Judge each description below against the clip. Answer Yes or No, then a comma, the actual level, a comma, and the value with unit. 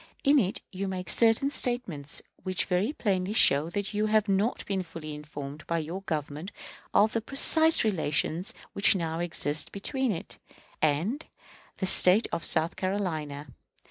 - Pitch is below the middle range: No, medium, 185 Hz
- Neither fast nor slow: Yes, average, 150 wpm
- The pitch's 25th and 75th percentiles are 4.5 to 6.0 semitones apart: Yes, average, 5.2 semitones